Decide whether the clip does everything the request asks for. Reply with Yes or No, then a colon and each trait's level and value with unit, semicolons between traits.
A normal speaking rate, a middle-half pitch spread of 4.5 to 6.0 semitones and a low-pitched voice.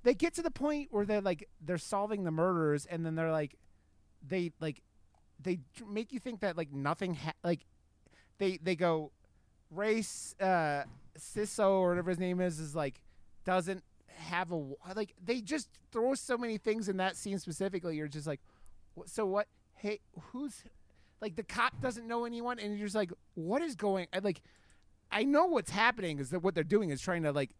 No: average, 195 wpm; average, 5.3 semitones; medium, 185 Hz